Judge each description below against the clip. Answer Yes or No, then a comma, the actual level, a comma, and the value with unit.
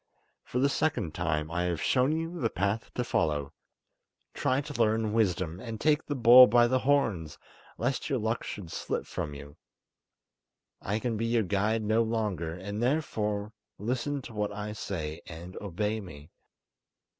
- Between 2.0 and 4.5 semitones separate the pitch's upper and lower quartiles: No, wide, 5.5 semitones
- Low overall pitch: Yes, low, 110 Hz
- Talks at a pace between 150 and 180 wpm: Yes, average, 160 wpm